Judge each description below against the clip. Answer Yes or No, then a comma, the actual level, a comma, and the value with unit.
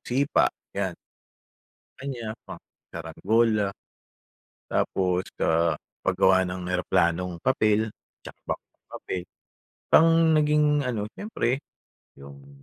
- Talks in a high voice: No, very low, 95 Hz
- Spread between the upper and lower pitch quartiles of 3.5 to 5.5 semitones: Yes, average, 5.0 semitones